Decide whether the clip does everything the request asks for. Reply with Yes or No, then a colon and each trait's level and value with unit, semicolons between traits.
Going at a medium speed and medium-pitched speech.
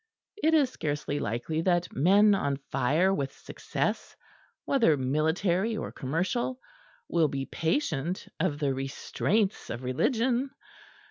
No: slow, 120 wpm; medium, 165 Hz